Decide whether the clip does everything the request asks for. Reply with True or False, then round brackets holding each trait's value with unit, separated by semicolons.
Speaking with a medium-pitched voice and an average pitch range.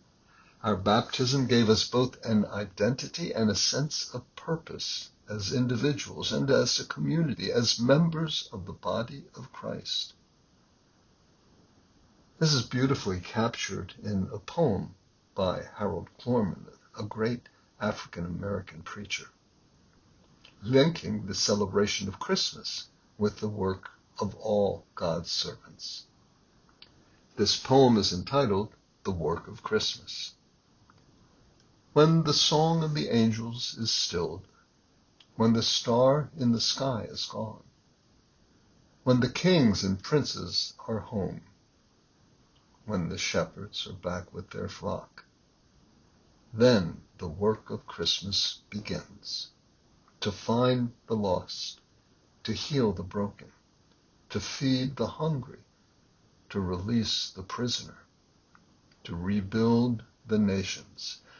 False (115 Hz; 4.1 semitones)